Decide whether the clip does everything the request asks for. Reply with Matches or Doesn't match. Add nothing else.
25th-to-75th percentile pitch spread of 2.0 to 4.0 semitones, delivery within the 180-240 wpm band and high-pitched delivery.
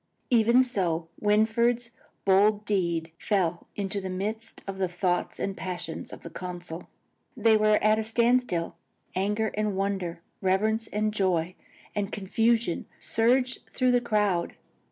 Doesn't match